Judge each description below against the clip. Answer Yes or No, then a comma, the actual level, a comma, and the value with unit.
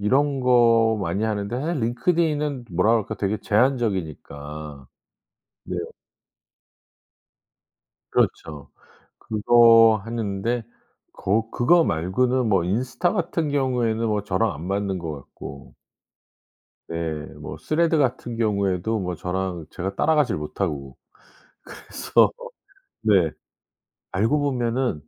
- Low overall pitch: Yes, low, 110 Hz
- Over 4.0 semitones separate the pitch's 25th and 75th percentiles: Yes, wide, 5.4 semitones